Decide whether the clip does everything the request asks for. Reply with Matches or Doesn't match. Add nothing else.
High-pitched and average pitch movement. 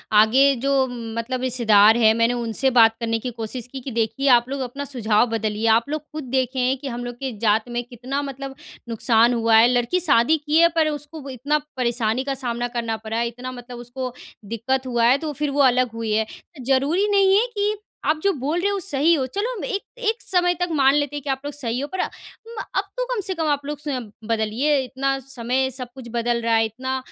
Matches